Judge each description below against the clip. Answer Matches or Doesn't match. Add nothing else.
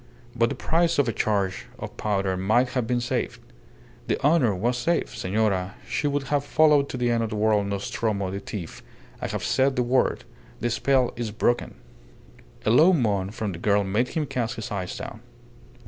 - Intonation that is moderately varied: Matches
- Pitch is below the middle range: Matches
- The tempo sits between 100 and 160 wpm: Doesn't match